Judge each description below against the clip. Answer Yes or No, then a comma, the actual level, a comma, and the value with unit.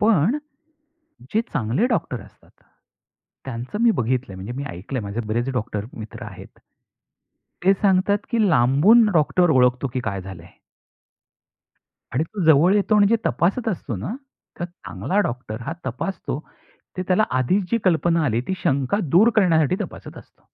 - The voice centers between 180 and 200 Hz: No, medium, 150 Hz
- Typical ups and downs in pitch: No, wide, 8.1 semitones